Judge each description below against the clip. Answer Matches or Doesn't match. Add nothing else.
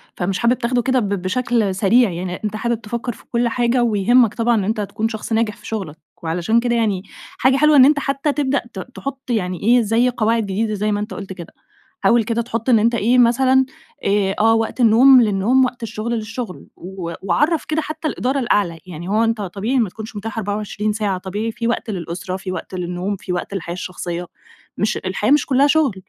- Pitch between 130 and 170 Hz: Doesn't match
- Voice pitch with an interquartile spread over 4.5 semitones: Doesn't match